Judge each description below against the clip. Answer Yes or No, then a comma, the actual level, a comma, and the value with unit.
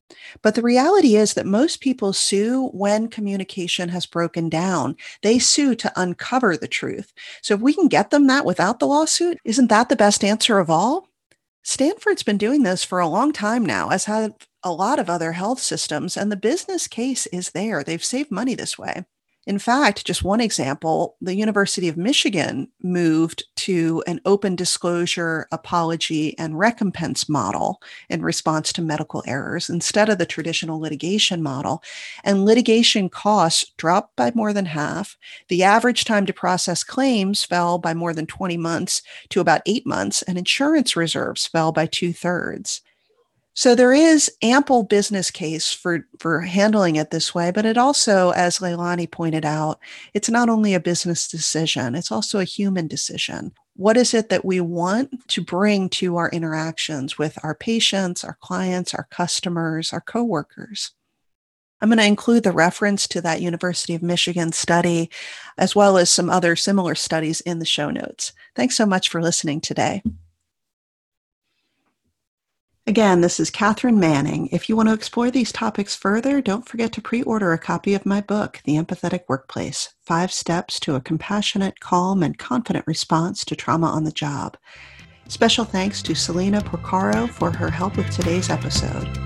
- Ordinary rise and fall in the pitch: Yes, average, 4.7 semitones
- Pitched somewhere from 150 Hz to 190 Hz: Yes, medium, 185 Hz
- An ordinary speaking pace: Yes, average, 170 wpm